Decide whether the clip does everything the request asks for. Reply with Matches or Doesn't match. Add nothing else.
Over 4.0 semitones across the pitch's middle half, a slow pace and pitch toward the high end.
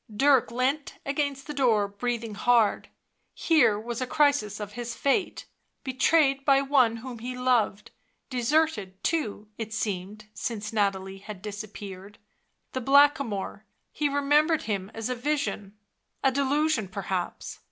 Matches